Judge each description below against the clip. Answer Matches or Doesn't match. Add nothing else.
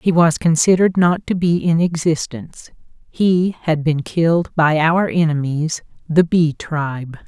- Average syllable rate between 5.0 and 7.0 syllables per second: Doesn't match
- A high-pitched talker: Doesn't match